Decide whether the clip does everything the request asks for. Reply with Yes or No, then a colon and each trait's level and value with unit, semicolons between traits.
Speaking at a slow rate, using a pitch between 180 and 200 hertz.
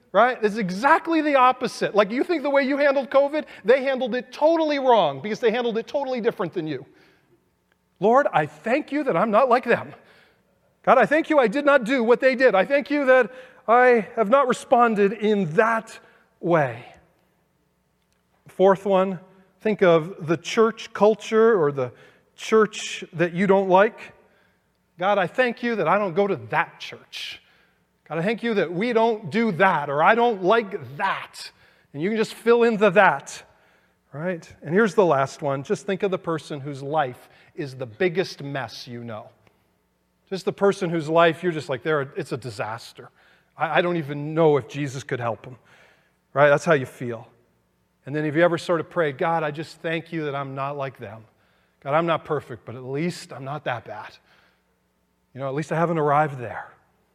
No: average, 195 wpm; medium, 185 Hz